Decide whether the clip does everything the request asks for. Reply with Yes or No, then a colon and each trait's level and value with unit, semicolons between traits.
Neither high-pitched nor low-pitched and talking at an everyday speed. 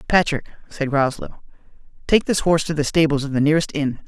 Yes: medium, 150 Hz; average, 190 wpm